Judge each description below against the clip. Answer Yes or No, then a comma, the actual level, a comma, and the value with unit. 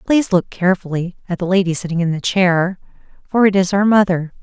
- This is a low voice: No, medium, 185 Hz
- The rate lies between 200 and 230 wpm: Yes, fast, 205 wpm